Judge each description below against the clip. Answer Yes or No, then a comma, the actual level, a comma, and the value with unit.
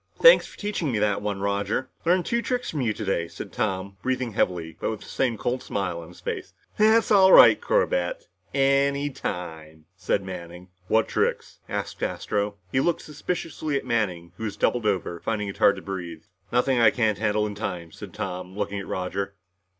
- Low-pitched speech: Yes, low, 105 Hz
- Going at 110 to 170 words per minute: No, average, 190 wpm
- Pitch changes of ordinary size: No, wide, 6.6 semitones